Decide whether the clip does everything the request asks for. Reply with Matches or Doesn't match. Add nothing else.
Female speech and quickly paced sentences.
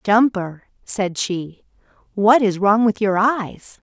Doesn't match